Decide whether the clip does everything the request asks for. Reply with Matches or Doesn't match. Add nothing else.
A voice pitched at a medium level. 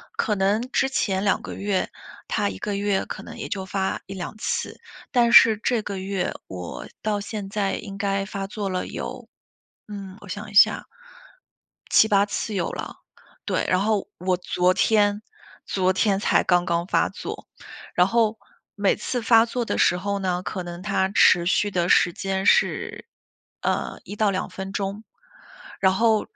Doesn't match